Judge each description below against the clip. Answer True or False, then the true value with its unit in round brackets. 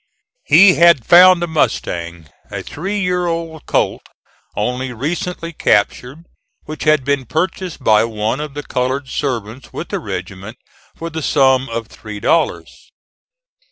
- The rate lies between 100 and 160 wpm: True (140 wpm)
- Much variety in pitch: True (6.3 semitones)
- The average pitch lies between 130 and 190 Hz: True (140 Hz)